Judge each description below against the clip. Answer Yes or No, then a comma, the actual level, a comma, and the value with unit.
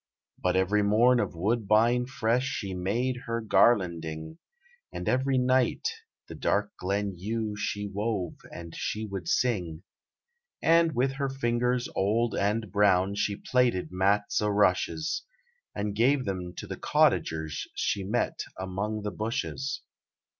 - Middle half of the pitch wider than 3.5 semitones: Yes, average, 4.2 semitones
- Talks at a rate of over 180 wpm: No, slow, 135 wpm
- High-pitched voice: No, low, 105 Hz